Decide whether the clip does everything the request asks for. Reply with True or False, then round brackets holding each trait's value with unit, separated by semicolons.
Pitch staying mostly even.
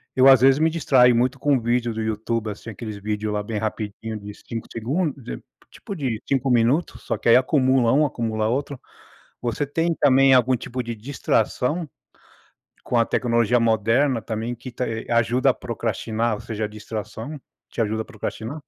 False (3.1 semitones)